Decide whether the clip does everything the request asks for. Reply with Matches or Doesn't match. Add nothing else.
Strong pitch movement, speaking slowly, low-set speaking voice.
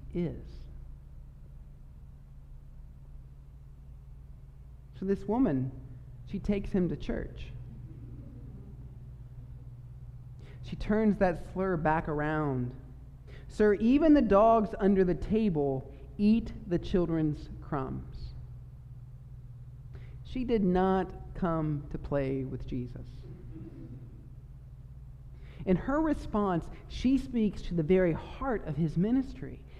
Matches